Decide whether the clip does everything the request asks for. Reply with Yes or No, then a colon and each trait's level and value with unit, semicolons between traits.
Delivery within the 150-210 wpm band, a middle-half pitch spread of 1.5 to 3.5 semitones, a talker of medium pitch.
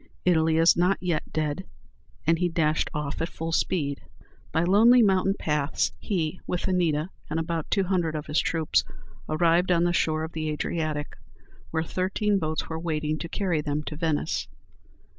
Yes: average, 170 wpm; narrow, 2.5 semitones; medium, 165 Hz